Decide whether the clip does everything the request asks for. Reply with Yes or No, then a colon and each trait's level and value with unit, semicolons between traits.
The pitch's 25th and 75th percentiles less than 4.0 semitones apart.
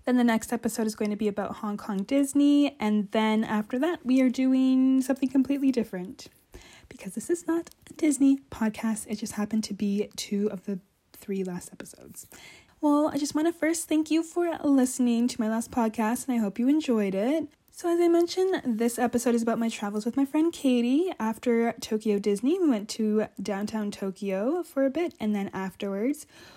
No: average, 5.1 semitones